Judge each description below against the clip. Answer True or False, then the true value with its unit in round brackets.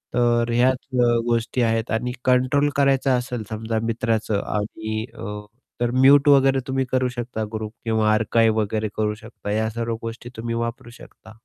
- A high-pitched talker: False (115 Hz)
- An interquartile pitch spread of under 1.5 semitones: False (2.4 semitones)